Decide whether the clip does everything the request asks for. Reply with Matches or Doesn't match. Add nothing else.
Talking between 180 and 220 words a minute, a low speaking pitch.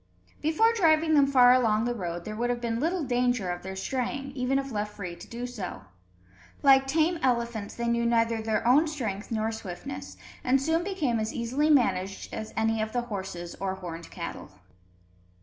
Doesn't match